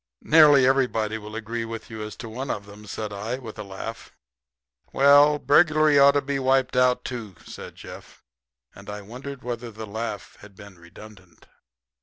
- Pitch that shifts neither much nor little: Yes, average, 4.2 semitones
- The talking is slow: No, average, 175 wpm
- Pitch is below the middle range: Yes, low, 115 Hz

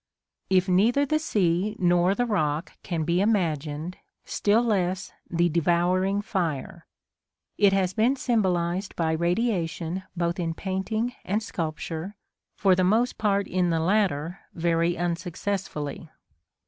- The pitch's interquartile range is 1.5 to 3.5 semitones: Yes, average, 3.2 semitones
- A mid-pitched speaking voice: Yes, medium, 180 Hz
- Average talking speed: No, slow, 125 wpm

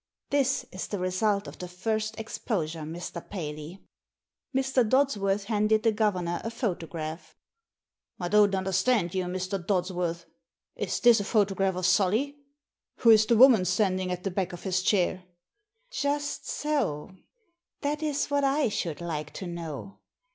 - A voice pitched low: No, high, 195 Hz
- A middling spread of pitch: Yes, average, 4.4 semitones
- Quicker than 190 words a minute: No, average, 155 wpm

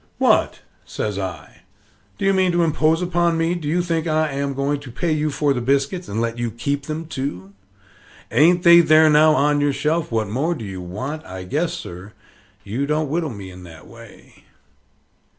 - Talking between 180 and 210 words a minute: Yes, average, 195 wpm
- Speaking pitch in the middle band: Yes, medium, 145 Hz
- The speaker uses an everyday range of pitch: No, wide, 5.9 semitones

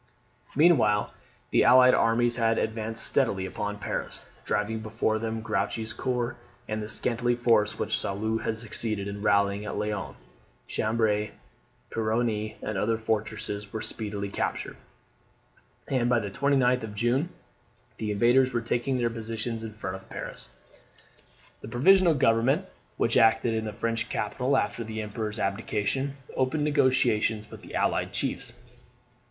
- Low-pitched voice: Yes, low, 110 Hz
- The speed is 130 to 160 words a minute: Yes, average, 140 wpm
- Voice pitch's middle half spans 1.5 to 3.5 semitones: Yes, narrow, 2.4 semitones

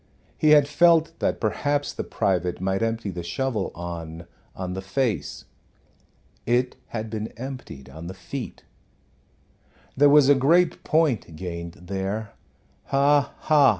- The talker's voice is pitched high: No, low, 115 Hz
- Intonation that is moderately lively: No, wide, 7.6 semitones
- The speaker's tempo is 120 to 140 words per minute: Yes, slow, 135 wpm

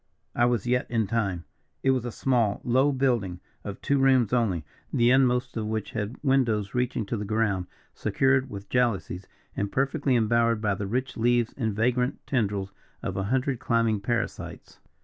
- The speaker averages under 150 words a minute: No, average, 170 wpm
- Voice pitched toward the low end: Yes, low, 115 Hz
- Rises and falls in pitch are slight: No, average, 3.4 semitones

